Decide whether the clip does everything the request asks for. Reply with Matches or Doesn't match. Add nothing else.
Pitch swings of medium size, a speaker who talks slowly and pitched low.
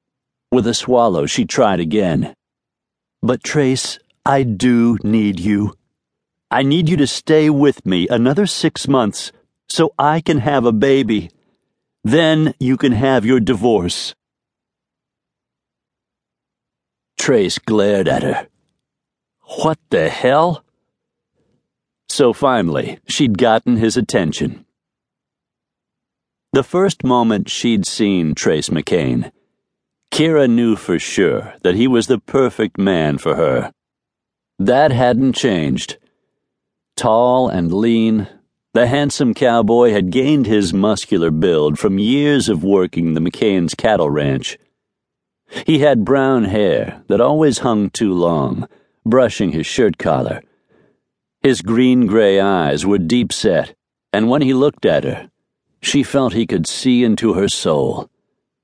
Matches